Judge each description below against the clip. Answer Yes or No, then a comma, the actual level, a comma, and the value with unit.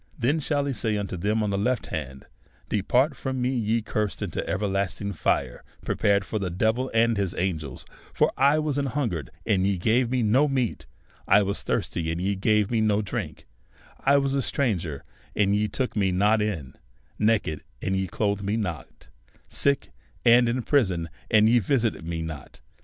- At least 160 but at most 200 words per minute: Yes, average, 185 wpm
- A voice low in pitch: Yes, low, 105 Hz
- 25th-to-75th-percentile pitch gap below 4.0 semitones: No, average, 4.3 semitones